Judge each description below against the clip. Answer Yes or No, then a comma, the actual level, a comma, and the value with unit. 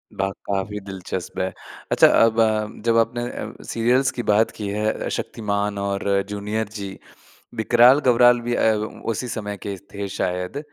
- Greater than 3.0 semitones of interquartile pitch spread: No, narrow, 2.6 semitones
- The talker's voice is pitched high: No, low, 105 Hz